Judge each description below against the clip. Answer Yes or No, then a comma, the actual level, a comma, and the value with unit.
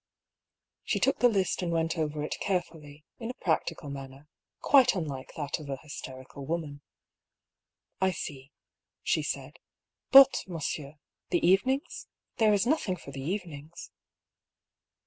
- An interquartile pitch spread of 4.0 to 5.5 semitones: Yes, average, 5.1 semitones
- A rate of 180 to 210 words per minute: No, slow, 135 wpm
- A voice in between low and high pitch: Yes, medium, 160 Hz